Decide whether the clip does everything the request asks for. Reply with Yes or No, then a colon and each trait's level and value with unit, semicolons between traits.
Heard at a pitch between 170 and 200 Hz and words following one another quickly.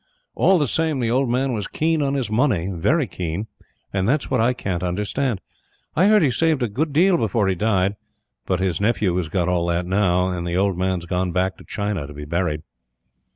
No: low, 100 Hz; fast, 215 wpm